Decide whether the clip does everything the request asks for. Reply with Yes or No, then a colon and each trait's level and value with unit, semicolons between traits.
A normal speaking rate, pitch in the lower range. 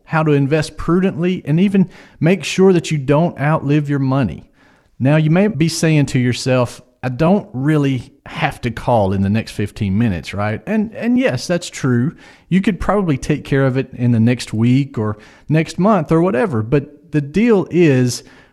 No: average, 190 wpm; medium, 145 Hz